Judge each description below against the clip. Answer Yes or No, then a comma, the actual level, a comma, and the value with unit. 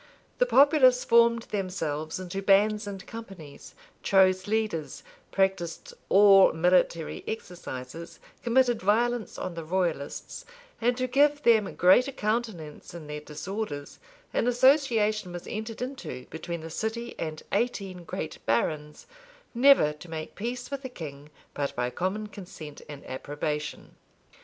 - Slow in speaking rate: Yes, slow, 130 wpm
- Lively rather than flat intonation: Yes, wide, 6.6 semitones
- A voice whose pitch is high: Yes, high, 195 Hz